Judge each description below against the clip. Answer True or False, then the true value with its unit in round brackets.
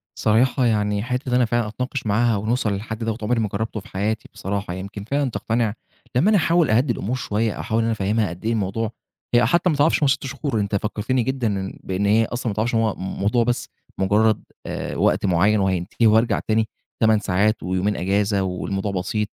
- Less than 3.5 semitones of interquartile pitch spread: True (3.0 semitones)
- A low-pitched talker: True (110 Hz)